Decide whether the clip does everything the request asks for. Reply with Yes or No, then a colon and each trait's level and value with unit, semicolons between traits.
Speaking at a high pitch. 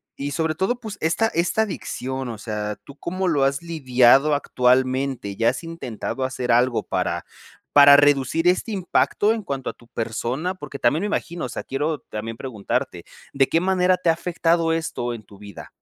No: medium, 140 Hz